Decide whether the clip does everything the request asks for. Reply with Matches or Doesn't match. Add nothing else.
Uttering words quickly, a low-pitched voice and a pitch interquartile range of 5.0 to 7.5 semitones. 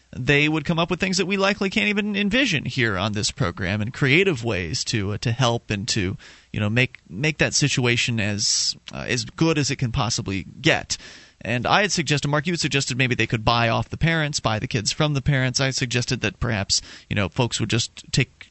Matches